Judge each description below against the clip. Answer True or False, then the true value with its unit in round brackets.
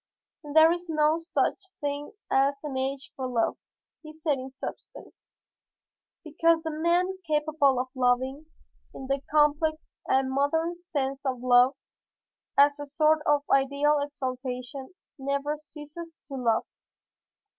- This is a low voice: False (285 Hz)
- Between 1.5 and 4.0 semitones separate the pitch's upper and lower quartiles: True (2.7 semitones)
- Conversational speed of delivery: False (130 wpm)